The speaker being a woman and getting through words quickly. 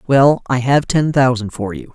Yes: female; fast, 215 wpm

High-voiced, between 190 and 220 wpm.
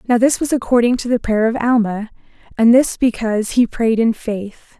Yes: high, 235 Hz; average, 200 wpm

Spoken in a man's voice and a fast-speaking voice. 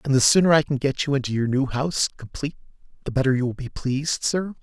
Yes: male; fast, 245 wpm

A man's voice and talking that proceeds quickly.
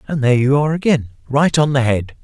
Yes: male; fast, 240 wpm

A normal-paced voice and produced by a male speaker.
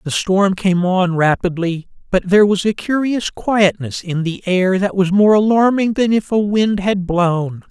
Yes: average, 185 wpm; male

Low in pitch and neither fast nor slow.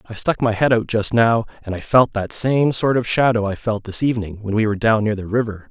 No: low, 110 Hz; fast, 275 wpm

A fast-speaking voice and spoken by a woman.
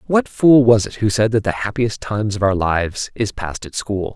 No: fast, 245 wpm; male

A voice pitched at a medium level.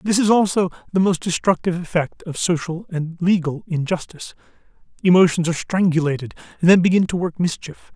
Yes: medium, 175 Hz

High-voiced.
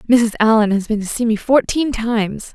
Yes: high, 225 Hz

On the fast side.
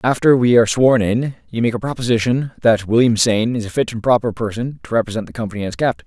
Yes: fast, 240 wpm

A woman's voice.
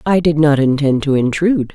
Yes: female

